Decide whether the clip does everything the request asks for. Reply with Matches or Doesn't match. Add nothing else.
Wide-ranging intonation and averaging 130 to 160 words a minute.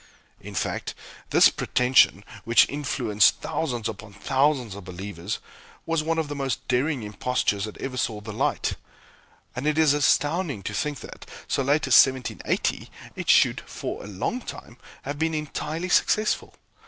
Matches